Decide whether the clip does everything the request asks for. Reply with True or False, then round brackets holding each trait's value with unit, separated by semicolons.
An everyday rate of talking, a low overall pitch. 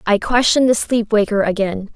False (185 wpm; 215 Hz)